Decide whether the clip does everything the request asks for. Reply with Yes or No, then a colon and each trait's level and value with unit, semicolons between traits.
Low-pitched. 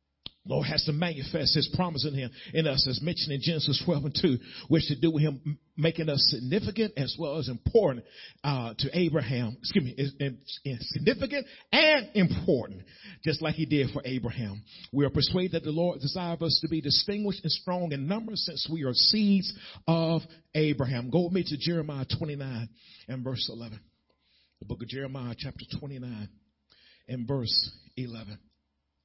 No: medium, 145 Hz